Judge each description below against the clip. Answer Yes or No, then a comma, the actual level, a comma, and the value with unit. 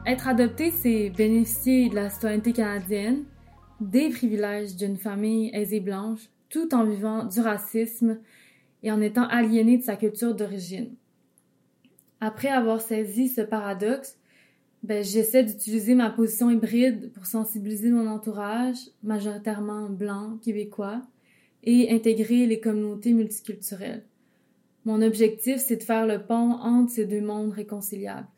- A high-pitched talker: Yes, high, 225 Hz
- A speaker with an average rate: No, slow, 130 wpm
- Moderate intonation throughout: No, narrow, 2.0 semitones